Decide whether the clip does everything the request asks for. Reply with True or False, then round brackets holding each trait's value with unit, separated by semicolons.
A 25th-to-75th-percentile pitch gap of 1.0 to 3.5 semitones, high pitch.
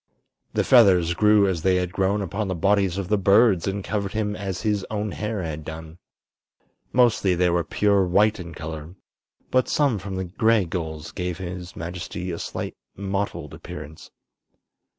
False (3.1 semitones; 95 Hz)